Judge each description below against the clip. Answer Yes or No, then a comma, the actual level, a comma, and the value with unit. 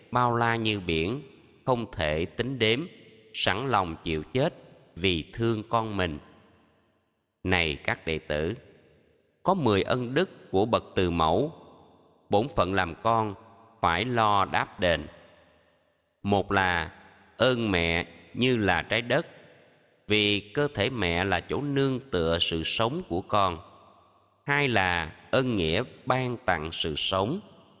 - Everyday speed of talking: No, slow, 140 wpm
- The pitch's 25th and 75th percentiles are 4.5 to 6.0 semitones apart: Yes, wide, 5.5 semitones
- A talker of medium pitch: No, low, 100 Hz